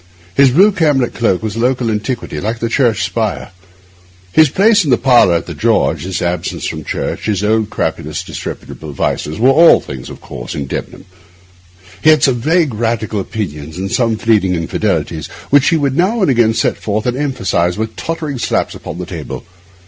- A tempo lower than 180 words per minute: No, average, 185 wpm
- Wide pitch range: Yes, wide, 6.4 semitones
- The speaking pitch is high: No, low, 115 Hz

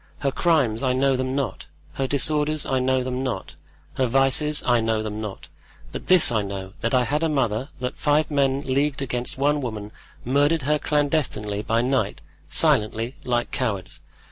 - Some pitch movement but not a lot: Yes, average, 3.9 semitones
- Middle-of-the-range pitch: No, low, 130 Hz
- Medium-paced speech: Yes, average, 170 wpm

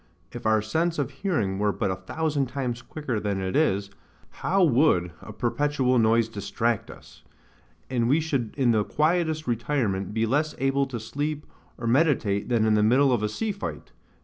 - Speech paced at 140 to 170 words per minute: No, average, 180 wpm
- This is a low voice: Yes, low, 120 Hz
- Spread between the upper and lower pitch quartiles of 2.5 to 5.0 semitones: No, wide, 5.4 semitones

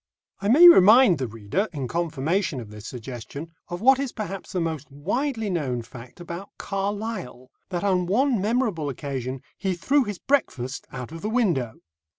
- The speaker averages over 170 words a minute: No, average, 165 wpm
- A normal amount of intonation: No, wide, 8.2 semitones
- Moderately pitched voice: Yes, medium, 175 Hz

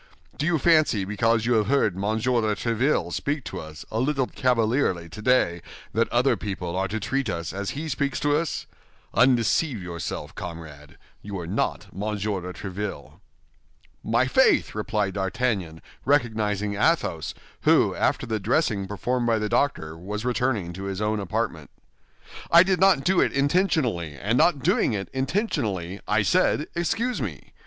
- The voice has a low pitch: Yes, low, 110 Hz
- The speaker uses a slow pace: No, average, 160 wpm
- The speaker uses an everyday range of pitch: No, wide, 5.8 semitones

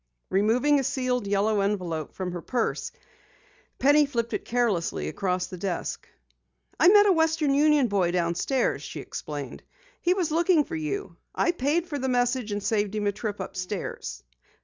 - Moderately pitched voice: No, high, 245 Hz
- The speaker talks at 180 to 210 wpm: No, average, 165 wpm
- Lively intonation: Yes, wide, 7.1 semitones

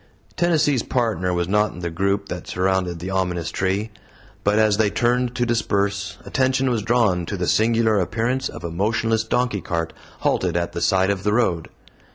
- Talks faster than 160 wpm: Yes, average, 185 wpm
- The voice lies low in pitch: Yes, low, 100 Hz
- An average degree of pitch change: Yes, average, 4.2 semitones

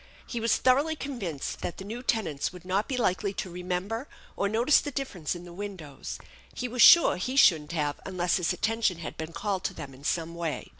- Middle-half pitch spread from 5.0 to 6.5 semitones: Yes, wide, 5.6 semitones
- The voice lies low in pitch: No, medium, 185 Hz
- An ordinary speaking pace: No, fast, 215 wpm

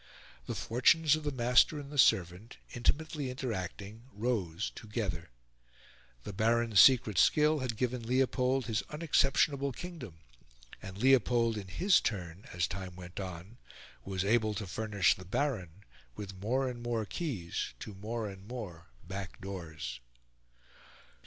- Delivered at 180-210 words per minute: No, slow, 135 wpm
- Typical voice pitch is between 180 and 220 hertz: No, low, 110 Hz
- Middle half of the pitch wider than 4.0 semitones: Yes, average, 5.2 semitones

